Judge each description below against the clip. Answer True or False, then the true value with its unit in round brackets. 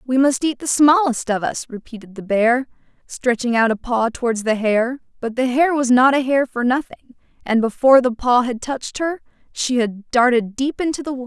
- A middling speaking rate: False (215 wpm)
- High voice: True (250 Hz)